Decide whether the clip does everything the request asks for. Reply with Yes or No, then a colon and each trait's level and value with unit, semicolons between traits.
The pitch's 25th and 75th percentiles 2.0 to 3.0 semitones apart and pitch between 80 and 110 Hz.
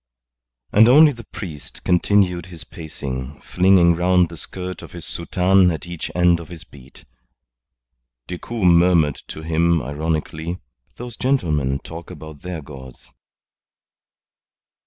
Yes: average, 2.7 semitones; very low, 85 Hz